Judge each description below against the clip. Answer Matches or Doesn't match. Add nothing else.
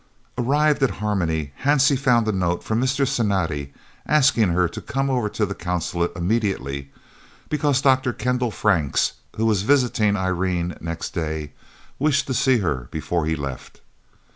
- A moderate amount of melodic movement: Doesn't match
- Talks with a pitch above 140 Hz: Doesn't match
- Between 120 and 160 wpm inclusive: Matches